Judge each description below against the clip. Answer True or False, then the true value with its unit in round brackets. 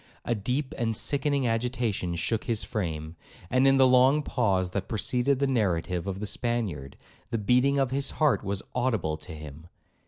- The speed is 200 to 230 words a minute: False (175 wpm)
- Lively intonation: True (5.7 semitones)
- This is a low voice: True (115 Hz)